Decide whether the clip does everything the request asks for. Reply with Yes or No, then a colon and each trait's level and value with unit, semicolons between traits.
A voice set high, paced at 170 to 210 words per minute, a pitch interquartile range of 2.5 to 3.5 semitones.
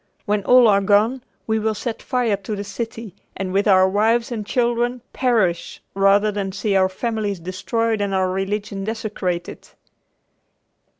No: high, 210 Hz; average, 155 wpm; average, 2.8 semitones